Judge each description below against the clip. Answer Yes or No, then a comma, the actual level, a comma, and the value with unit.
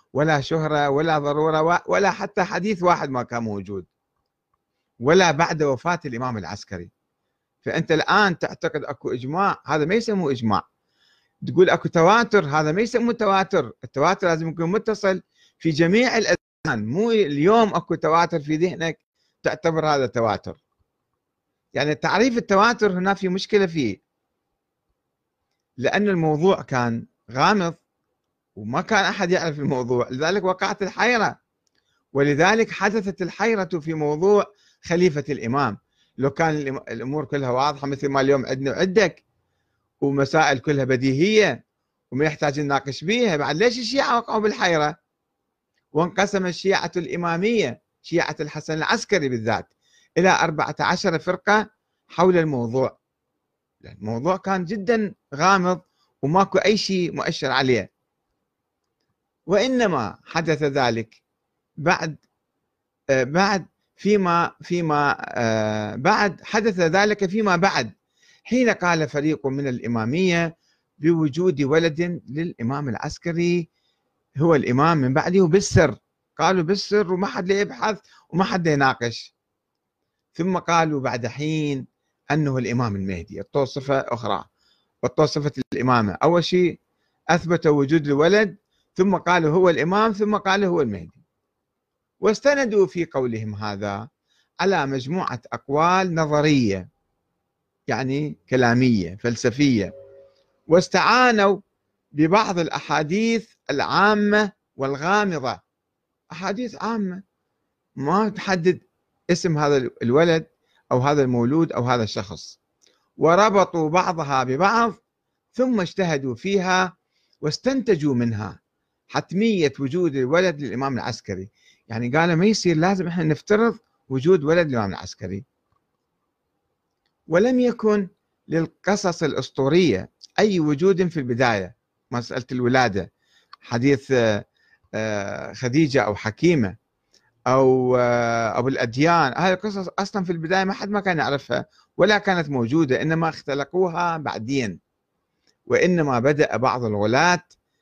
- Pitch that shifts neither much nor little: No, wide, 6.2 semitones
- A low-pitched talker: No, medium, 160 Hz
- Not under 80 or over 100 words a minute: No, average, 110 wpm